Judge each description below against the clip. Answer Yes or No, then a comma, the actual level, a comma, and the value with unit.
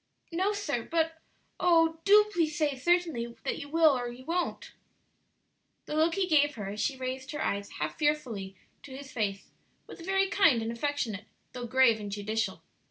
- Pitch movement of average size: No, wide, 6.1 semitones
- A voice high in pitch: Yes, very high, 285 Hz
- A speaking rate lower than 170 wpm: No, average, 175 wpm